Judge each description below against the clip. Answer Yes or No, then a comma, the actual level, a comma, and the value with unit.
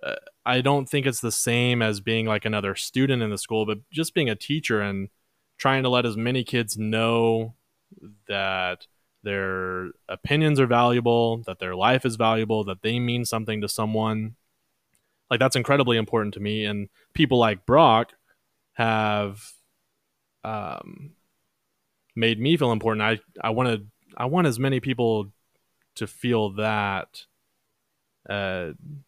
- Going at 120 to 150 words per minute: Yes, average, 145 wpm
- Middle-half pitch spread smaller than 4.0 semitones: Yes, average, 3.2 semitones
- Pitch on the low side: Yes, low, 115 Hz